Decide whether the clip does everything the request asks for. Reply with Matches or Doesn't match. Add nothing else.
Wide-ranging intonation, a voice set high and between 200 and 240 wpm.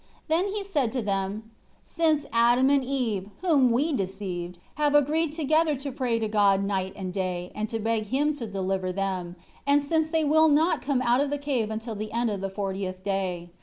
Matches